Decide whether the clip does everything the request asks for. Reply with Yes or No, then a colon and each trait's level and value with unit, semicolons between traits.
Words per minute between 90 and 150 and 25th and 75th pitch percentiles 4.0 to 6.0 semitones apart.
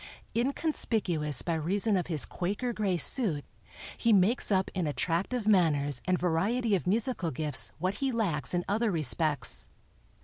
Yes: average, 145 wpm; wide, 5.5 semitones